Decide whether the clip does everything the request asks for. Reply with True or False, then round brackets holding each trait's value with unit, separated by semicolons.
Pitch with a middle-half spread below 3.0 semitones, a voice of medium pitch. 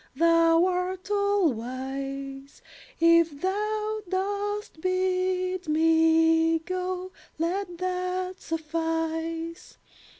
False (2.4 semitones; 335 Hz)